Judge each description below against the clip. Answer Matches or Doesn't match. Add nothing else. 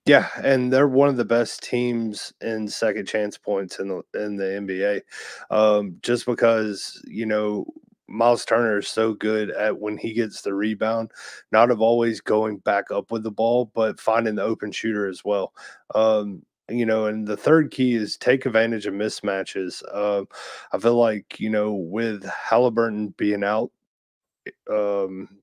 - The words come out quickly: Doesn't match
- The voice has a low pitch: Matches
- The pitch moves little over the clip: Matches